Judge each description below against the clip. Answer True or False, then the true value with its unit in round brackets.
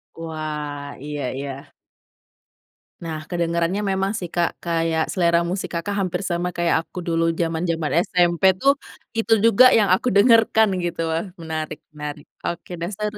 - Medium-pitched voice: True (170 Hz)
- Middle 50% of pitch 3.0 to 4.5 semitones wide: False (2.6 semitones)